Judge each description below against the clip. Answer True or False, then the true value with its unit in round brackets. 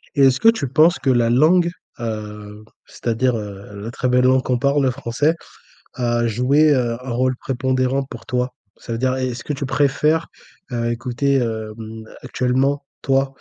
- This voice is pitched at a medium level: False (125 Hz)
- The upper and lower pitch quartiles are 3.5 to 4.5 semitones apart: False (2.8 semitones)